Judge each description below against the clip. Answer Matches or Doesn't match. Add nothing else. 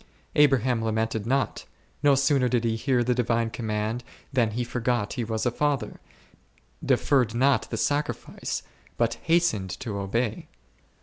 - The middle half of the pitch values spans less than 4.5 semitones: Matches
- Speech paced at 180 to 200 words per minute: Doesn't match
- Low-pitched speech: Matches